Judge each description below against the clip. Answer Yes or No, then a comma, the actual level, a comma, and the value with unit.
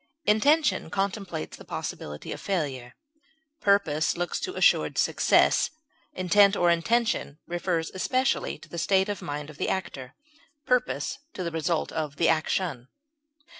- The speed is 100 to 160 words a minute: Yes, slow, 135 wpm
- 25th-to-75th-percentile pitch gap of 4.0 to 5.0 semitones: Yes, average, 4.5 semitones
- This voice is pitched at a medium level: Yes, medium, 175 Hz